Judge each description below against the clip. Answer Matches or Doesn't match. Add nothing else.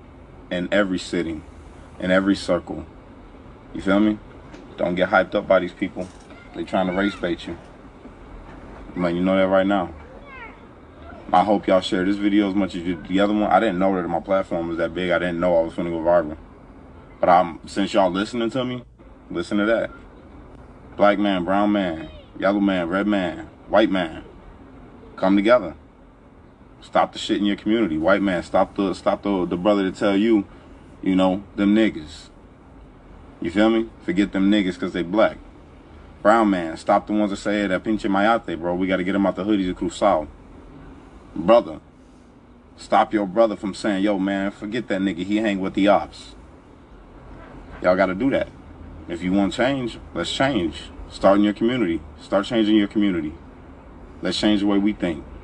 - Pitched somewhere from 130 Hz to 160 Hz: Doesn't match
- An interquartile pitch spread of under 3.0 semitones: Matches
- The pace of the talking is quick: Doesn't match